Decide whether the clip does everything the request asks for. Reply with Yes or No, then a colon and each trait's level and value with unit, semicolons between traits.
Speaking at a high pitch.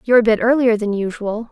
Yes: high, 225 Hz